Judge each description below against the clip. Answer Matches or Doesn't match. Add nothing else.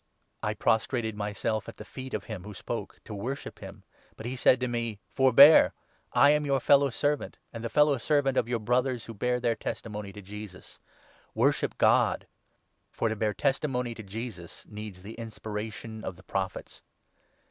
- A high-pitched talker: Doesn't match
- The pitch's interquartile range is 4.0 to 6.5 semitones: Doesn't match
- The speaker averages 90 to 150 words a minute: Doesn't match